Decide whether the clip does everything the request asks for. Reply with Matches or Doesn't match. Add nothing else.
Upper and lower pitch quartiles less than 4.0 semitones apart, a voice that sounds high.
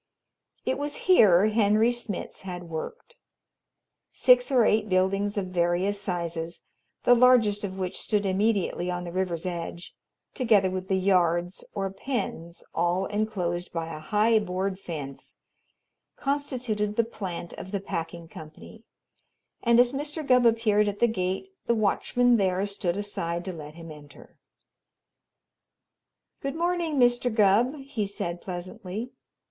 Doesn't match